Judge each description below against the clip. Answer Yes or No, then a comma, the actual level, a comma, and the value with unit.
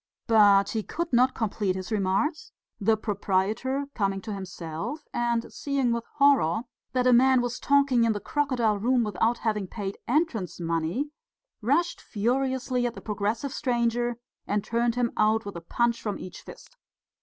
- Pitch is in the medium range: No, high, 230 Hz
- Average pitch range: Yes, average, 4.0 semitones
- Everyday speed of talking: Yes, average, 160 wpm